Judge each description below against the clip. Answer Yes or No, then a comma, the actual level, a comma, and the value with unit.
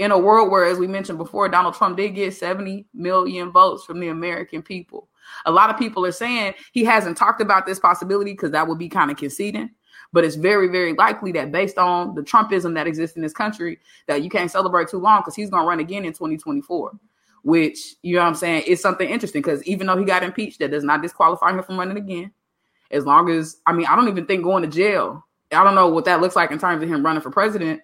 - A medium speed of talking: No, fast, 250 wpm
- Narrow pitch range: No, average, 3.0 semitones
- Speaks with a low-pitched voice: No, medium, 185 Hz